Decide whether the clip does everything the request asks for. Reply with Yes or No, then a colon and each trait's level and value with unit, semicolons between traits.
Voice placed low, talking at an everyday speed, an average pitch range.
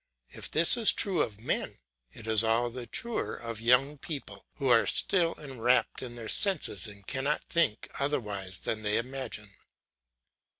Yes: low, 120 Hz; average, 160 wpm; average, 4.9 semitones